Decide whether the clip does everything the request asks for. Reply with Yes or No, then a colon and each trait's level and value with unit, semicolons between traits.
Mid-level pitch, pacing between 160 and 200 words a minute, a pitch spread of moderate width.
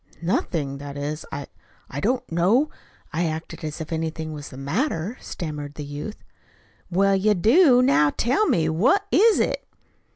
No: medium, 165 Hz; average, 165 wpm; wide, 7.2 semitones